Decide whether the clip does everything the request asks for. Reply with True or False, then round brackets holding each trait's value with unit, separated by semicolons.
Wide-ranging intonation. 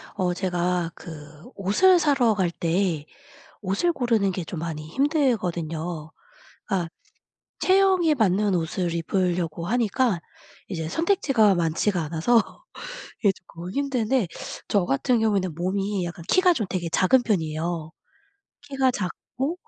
True (6.4 semitones)